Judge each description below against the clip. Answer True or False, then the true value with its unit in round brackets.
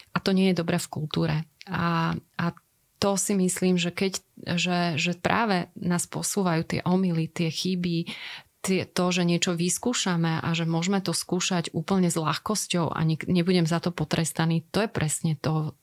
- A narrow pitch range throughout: True (2.0 semitones)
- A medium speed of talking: False (175 wpm)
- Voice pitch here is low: False (175 Hz)